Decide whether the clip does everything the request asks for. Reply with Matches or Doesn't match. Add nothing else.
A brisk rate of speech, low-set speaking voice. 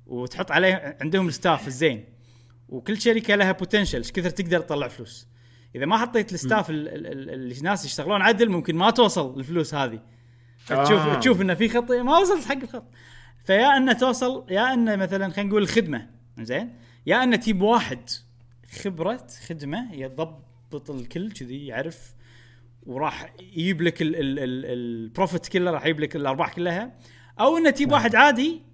Doesn't match